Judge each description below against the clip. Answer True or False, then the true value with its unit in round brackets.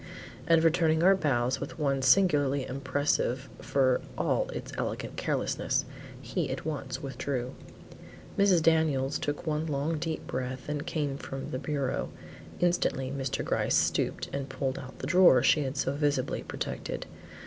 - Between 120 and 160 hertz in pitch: True (140 Hz)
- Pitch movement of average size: True (3.1 semitones)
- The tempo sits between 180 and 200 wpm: False (150 wpm)